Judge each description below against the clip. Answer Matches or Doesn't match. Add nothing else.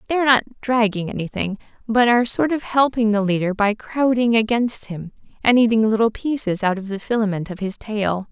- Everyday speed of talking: Matches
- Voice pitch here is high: Matches